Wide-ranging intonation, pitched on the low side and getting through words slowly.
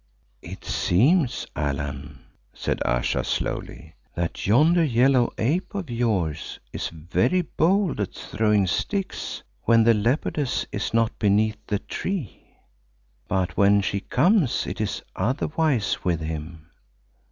Yes: wide, 7.9 semitones; low, 110 Hz; slow, 120 wpm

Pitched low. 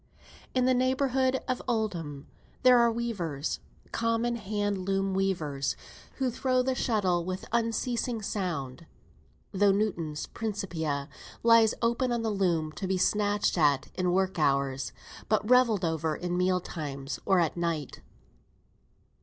No: high, 195 Hz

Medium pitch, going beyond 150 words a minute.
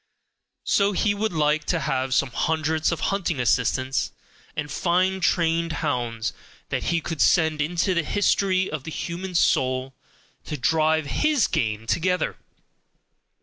No: medium, 160 Hz; average, 140 wpm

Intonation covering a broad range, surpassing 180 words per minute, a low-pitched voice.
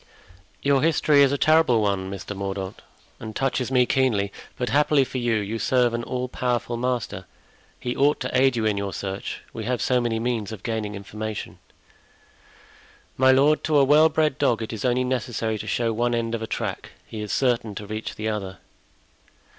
No: average, 3.3 semitones; average, 195 wpm; low, 120 Hz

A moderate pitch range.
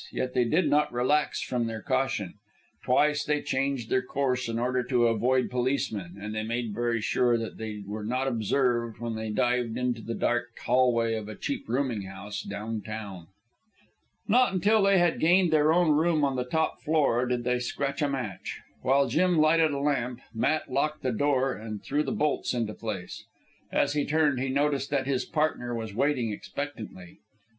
Yes: average, 4.1 semitones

